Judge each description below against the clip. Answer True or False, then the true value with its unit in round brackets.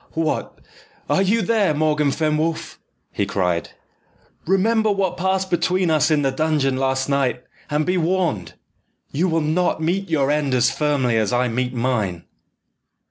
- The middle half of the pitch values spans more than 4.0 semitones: True (5.3 semitones)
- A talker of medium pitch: True (155 Hz)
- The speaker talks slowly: False (150 wpm)